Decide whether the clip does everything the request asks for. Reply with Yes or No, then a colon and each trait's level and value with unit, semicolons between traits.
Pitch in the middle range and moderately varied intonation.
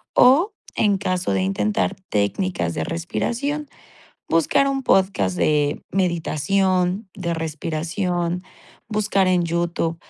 Yes: medium, 180 Hz; average, 3.5 semitones